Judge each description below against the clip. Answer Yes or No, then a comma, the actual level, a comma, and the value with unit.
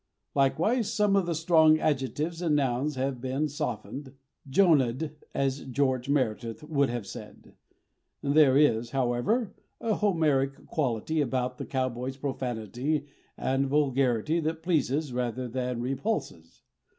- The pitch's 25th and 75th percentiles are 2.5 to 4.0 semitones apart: Yes, average, 3.7 semitones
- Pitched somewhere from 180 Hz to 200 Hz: No, low, 135 Hz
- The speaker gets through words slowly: Yes, slow, 125 wpm